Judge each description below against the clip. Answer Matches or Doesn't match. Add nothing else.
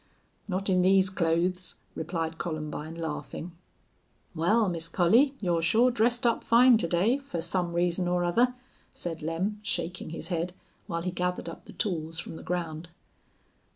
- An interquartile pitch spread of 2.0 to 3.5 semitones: Matches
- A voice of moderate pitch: Matches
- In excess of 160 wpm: Doesn't match